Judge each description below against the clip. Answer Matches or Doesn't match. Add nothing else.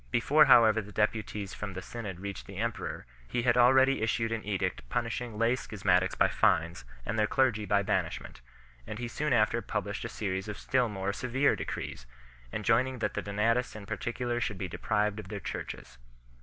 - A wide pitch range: Doesn't match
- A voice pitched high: Doesn't match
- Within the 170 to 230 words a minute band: Matches